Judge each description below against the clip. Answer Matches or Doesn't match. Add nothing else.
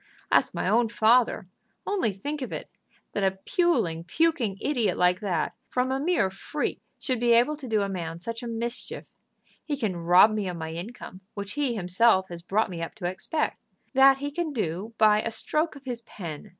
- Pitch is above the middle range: Matches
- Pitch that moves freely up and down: Matches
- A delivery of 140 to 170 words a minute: Doesn't match